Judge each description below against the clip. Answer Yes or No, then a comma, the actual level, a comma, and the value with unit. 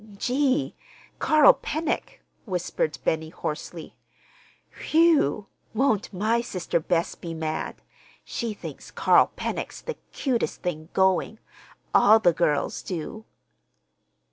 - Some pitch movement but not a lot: No, wide, 7.2 semitones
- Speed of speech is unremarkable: No, slow, 105 wpm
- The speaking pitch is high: Yes, high, 195 Hz